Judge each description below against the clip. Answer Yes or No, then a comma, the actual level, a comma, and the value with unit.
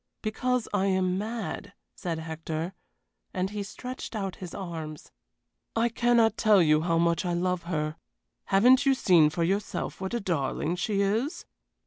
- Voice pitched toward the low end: No, high, 190 Hz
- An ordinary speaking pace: Yes, average, 155 wpm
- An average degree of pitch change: Yes, average, 4.6 semitones